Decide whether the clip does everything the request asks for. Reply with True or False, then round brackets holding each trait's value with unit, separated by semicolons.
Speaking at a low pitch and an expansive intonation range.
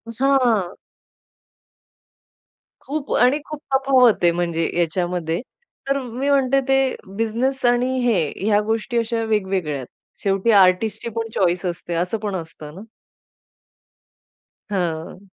False (220 Hz; 6.0 semitones)